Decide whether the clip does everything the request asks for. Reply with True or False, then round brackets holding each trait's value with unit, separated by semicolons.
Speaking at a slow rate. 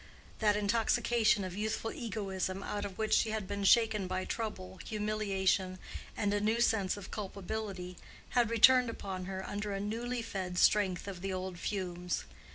False (165 wpm)